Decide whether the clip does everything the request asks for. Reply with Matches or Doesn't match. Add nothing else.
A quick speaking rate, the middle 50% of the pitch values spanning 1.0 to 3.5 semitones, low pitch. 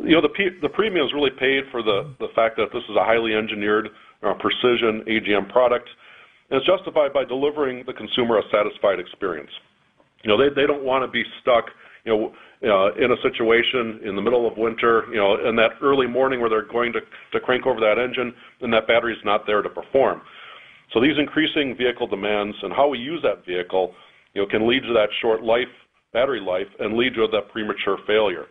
Matches